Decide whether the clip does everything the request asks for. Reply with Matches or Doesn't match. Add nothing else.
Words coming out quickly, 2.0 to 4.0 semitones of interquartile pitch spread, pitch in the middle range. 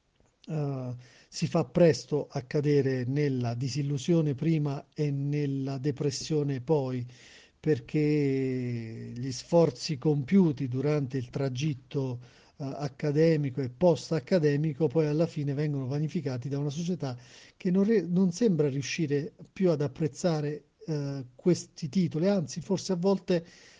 Doesn't match